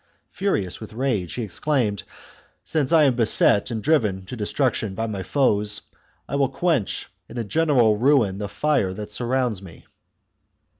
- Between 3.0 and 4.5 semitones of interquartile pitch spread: No, average, 5.1 semitones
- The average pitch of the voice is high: No, low, 115 Hz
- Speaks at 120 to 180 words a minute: Yes, average, 155 wpm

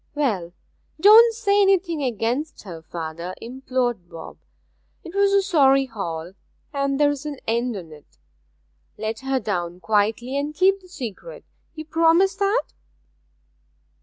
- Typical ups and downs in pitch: No, wide, 8.7 semitones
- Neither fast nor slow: No, slow, 125 wpm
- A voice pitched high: Yes, very high, 270 Hz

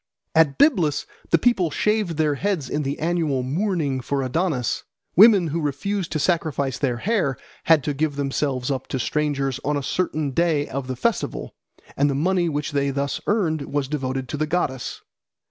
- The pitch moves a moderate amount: Yes, average, 3.8 semitones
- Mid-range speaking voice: Yes, medium, 150 Hz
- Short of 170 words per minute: No, average, 180 wpm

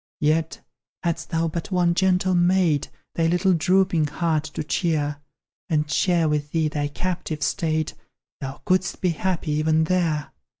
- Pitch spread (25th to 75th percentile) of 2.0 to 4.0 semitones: Yes, average, 2.9 semitones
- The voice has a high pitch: No, medium, 165 Hz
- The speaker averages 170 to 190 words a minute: No, average, 145 wpm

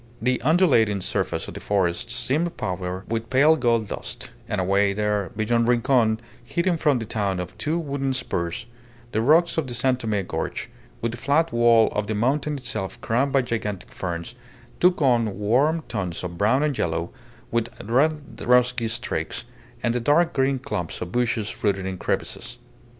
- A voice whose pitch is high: No, low, 120 Hz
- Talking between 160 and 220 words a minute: Yes, average, 170 wpm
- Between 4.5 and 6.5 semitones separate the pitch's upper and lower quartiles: Yes, average, 4.9 semitones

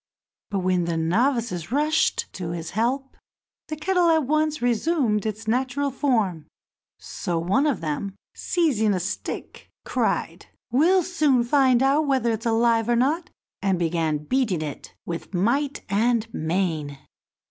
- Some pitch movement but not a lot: No, wide, 7.4 semitones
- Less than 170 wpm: Yes, average, 140 wpm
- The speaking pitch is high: Yes, high, 235 Hz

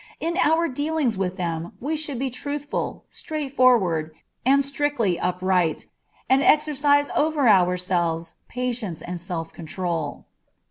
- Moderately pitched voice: No, high, 240 Hz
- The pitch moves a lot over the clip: Yes, wide, 8.4 semitones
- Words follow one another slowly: Yes, slow, 120 wpm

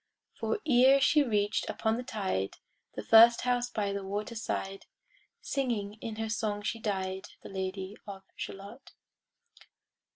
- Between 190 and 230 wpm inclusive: No, average, 140 wpm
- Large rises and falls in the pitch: No, average, 3.1 semitones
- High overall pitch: Yes, high, 215 Hz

